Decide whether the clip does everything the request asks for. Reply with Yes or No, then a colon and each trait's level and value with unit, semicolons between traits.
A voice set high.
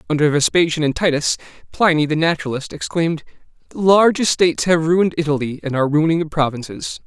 No: medium, 160 Hz